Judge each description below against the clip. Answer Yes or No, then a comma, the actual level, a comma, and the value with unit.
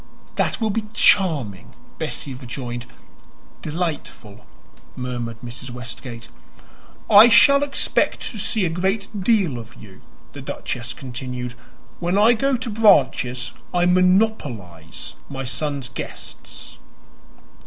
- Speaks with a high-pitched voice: No, medium, 140 Hz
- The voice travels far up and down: Yes, wide, 8.9 semitones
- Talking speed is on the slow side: Yes, slow, 110 wpm